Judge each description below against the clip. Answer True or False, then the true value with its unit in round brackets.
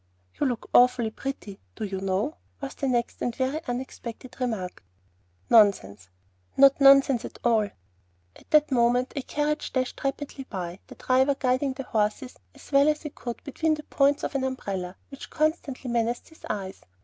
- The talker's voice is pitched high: True (255 Hz)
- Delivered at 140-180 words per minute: True (170 wpm)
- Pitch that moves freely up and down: False (3.8 semitones)